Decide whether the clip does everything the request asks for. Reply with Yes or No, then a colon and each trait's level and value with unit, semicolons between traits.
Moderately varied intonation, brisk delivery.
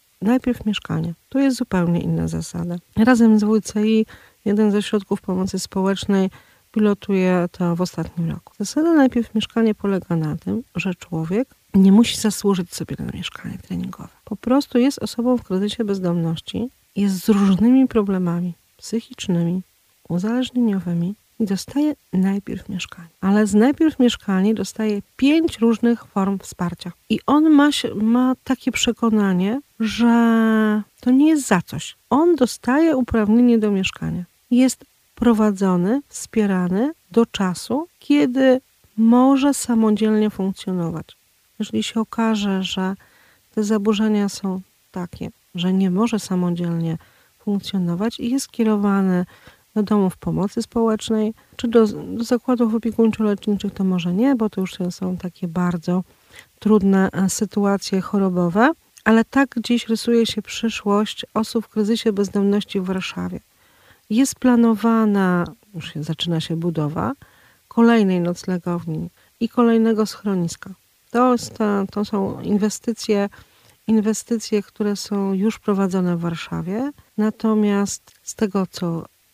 No: average, 3.7 semitones; average, 125 wpm